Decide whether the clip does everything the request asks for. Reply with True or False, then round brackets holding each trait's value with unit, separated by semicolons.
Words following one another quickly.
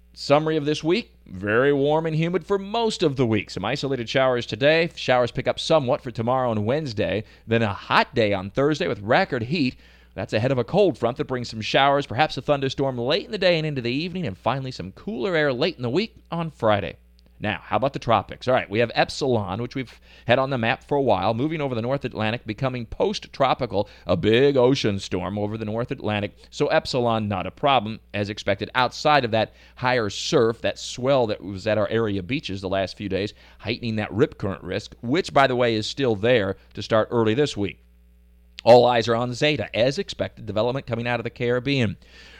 True (220 wpm)